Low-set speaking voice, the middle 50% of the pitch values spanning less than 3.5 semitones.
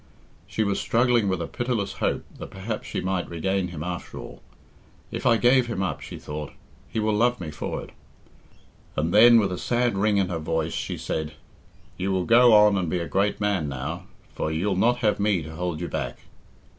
No: very low, 95 Hz; average, 4.6 semitones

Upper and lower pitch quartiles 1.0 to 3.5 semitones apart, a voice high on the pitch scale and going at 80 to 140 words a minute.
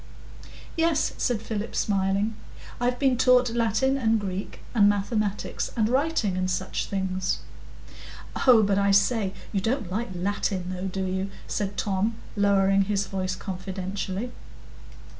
Yes: average, 3.0 semitones; high, 200 Hz; slow, 135 wpm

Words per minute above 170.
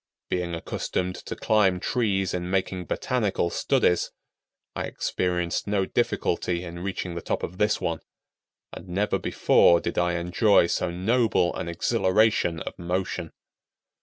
No: slow, 135 wpm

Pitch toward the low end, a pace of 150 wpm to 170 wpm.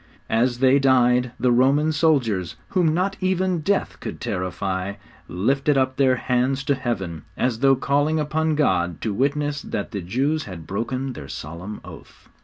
Yes: low, 130 Hz; average, 160 wpm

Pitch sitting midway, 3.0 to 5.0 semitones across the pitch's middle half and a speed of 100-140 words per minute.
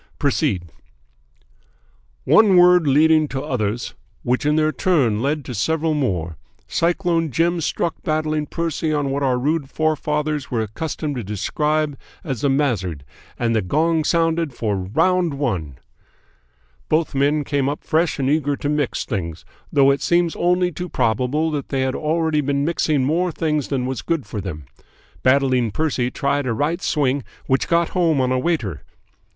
No: medium, 145 Hz; average, 3.9 semitones; average, 160 wpm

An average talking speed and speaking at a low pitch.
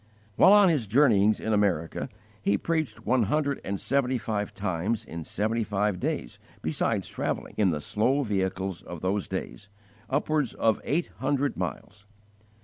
Yes: average, 150 wpm; low, 105 Hz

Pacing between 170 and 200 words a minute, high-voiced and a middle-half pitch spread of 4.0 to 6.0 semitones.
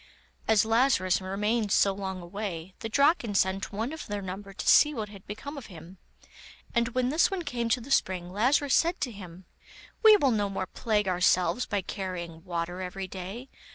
Yes: average, 190 wpm; high, 205 Hz; average, 4.5 semitones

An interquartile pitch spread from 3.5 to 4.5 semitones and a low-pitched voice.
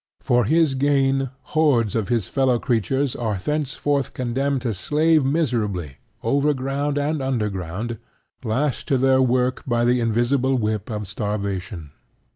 Yes: average, 4.2 semitones; low, 125 Hz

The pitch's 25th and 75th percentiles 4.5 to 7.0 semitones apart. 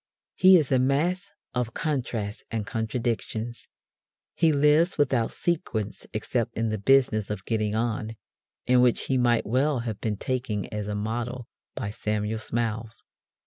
No: average, 3.4 semitones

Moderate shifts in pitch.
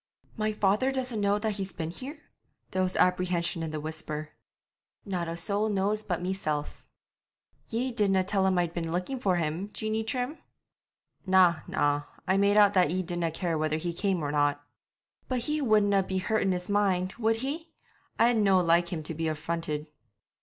Yes: average, 4.1 semitones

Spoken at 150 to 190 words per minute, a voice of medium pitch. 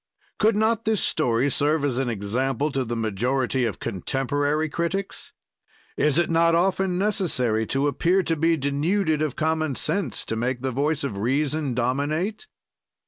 Yes: average, 155 wpm; medium, 145 Hz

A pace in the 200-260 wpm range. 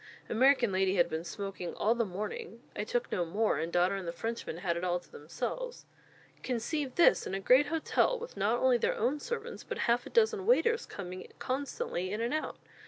Yes: fast, 205 wpm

